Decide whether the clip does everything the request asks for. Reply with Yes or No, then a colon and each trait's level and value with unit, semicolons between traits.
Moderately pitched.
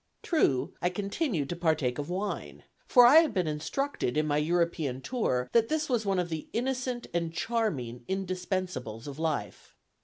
Yes: medium, 175 Hz